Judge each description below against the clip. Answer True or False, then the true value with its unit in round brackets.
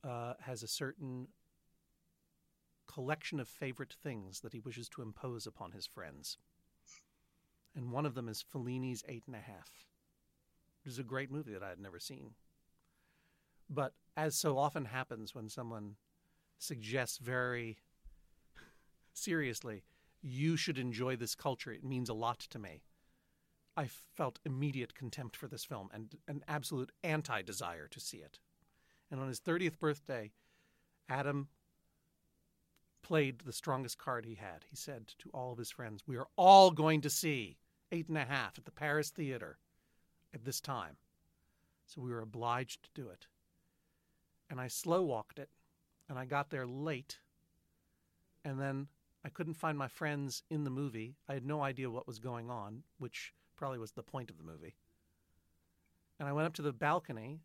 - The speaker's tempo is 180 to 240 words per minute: False (165 wpm)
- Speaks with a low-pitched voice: True (130 Hz)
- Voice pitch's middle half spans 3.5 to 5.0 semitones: True (4.7 semitones)